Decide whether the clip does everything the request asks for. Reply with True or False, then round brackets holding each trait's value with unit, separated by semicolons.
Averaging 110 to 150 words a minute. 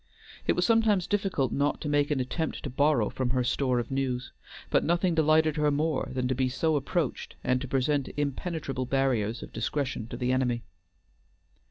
False (185 wpm)